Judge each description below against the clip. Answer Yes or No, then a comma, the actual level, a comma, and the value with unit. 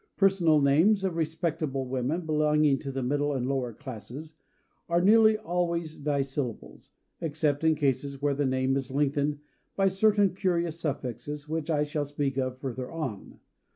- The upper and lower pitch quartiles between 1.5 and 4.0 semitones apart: Yes, average, 3.5 semitones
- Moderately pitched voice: Yes, medium, 150 Hz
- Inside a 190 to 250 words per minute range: No, average, 155 wpm